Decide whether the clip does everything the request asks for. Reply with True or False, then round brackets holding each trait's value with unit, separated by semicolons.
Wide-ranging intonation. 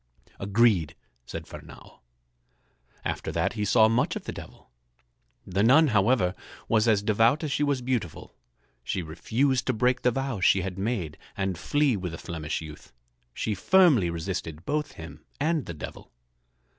True (6.2 semitones)